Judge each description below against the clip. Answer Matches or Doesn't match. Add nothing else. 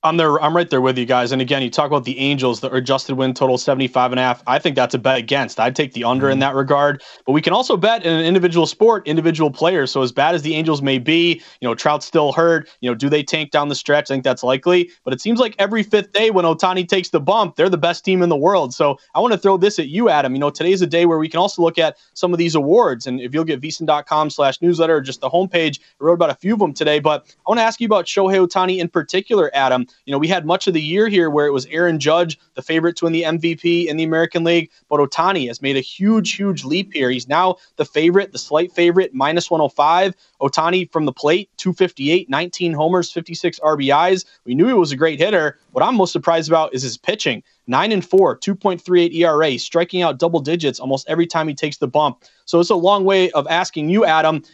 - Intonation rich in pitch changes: Doesn't match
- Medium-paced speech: Doesn't match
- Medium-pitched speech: Matches